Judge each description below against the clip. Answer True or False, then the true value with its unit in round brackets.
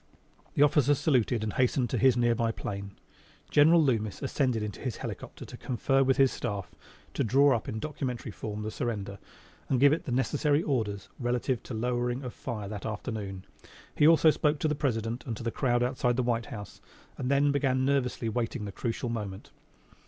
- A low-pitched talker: True (125 Hz)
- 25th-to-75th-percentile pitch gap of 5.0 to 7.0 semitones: False (3.7 semitones)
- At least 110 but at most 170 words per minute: False (190 wpm)